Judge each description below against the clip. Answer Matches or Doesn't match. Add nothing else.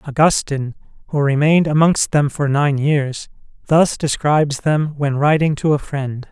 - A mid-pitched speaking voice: Matches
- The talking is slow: Doesn't match